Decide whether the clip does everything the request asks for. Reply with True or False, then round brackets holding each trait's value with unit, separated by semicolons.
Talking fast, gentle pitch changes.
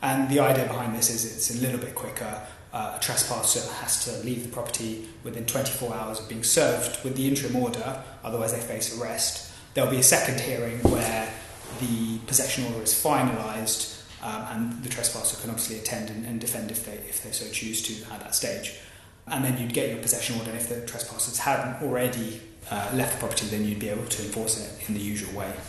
True (215 wpm; 1.9 semitones)